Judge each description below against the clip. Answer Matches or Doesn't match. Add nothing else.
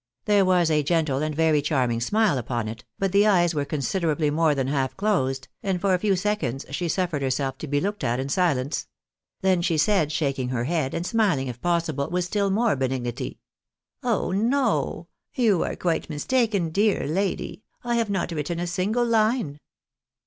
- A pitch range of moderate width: Doesn't match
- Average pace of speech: Matches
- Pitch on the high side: Doesn't match